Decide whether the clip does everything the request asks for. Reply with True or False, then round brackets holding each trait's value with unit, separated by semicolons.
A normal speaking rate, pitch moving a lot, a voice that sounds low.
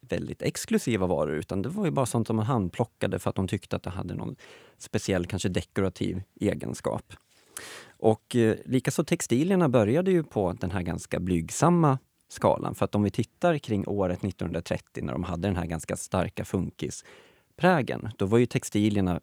True (175 wpm; 5.8 semitones; 105 Hz)